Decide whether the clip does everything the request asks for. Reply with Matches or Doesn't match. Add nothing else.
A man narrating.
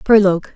Doesn't match